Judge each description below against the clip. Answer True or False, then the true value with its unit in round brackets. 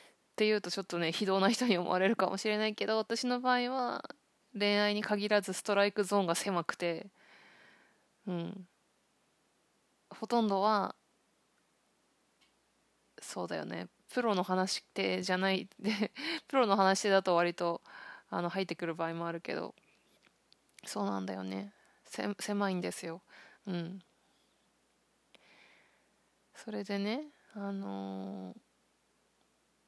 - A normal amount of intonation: True (3.6 semitones)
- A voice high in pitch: True (195 Hz)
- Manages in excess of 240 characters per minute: False (235 characters per minute)